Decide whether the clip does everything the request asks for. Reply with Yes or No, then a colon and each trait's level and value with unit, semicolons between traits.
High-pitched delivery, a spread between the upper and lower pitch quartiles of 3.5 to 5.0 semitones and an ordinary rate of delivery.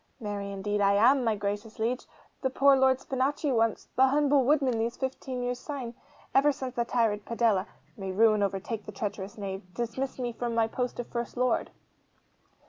Yes: high, 235 Hz; average, 4.0 semitones; average, 180 wpm